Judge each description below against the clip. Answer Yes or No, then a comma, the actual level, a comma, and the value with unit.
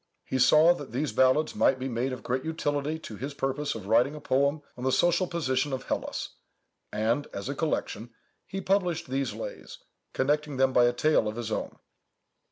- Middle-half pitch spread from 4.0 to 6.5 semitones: No, average, 3.1 semitones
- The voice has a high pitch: No, low, 135 Hz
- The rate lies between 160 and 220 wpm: Yes, average, 190 wpm